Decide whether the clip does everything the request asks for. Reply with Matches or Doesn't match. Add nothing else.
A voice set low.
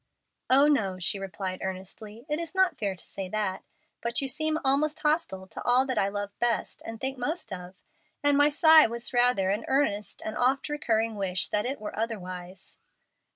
Doesn't match